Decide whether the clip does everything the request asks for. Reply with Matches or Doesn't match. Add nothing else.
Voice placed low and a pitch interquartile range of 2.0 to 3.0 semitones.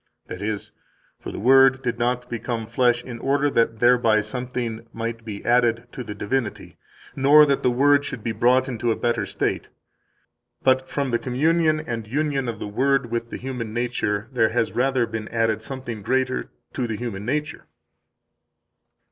Matches